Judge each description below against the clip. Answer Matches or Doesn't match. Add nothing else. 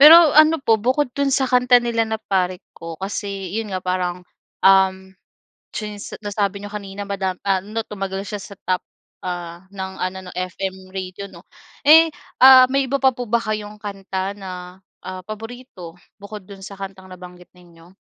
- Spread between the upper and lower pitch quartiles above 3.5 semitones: Doesn't match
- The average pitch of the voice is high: Matches